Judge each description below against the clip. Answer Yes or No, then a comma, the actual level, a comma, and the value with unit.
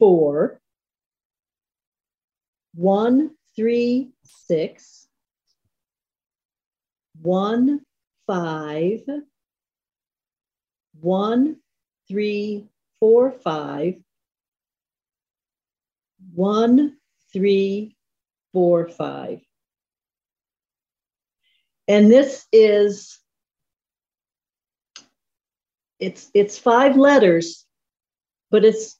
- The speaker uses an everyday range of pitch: No, wide, 5.7 semitones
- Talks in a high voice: Yes, high, 210 Hz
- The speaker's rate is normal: No, slow, 50 wpm